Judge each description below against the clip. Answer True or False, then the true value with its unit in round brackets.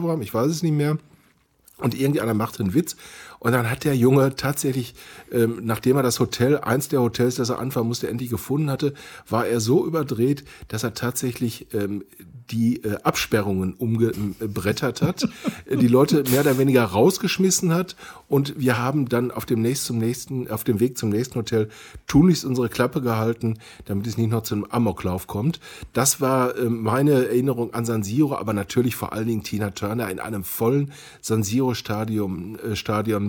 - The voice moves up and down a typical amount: True (3.5 semitones)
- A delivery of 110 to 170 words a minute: False (180 wpm)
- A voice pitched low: True (120 Hz)